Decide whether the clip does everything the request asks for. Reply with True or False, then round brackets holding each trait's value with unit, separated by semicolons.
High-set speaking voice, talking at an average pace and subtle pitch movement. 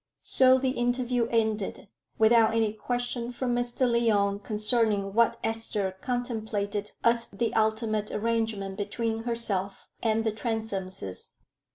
False (225 Hz; 115 wpm; 2.2 semitones)